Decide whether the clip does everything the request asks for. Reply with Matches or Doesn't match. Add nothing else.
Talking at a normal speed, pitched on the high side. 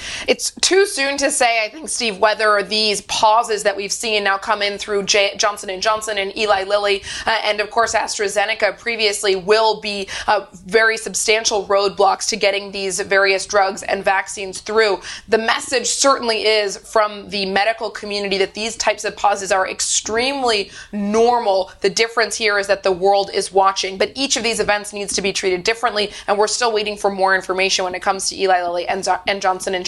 Matches